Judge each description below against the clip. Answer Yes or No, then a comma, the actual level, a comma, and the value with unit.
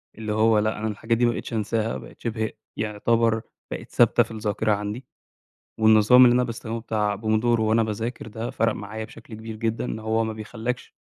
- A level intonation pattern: Yes, narrow, 1.1 semitones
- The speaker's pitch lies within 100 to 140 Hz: Yes, low, 110 Hz